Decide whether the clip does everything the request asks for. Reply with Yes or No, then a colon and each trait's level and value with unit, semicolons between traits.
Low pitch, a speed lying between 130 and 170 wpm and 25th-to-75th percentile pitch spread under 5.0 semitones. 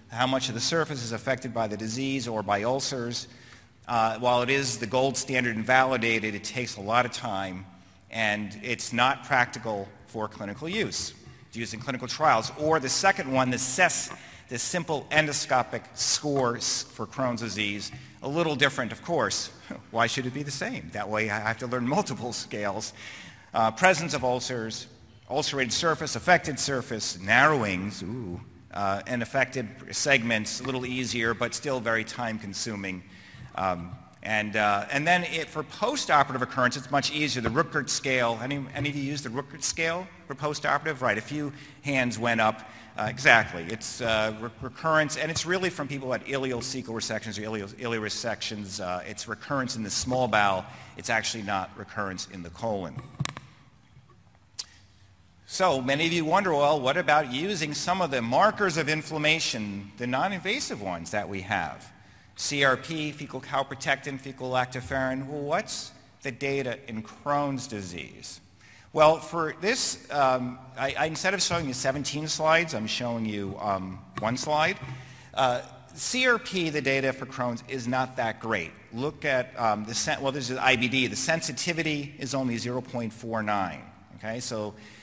Yes: low, 125 Hz; average, 165 wpm; average, 4.4 semitones